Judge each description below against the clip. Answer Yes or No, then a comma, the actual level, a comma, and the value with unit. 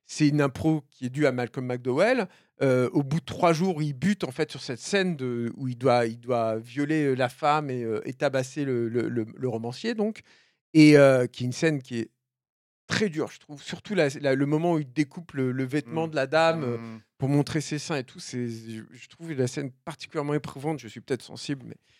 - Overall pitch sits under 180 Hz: Yes, medium, 140 Hz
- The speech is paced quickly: Yes, fast, 235 wpm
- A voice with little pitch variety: No, average, 3.8 semitones